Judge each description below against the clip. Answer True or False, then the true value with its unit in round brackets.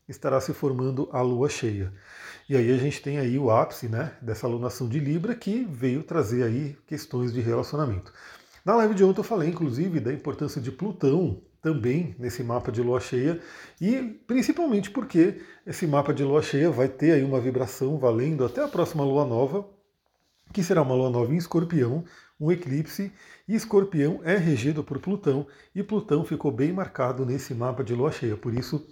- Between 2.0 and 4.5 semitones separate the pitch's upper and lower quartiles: False (5.1 semitones)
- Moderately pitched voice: True (145 Hz)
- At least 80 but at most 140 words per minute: False (185 wpm)